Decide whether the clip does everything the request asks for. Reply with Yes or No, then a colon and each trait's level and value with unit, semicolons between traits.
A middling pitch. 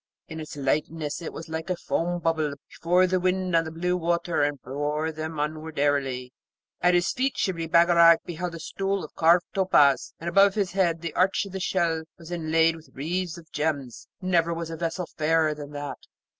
Yes: medium, 165 Hz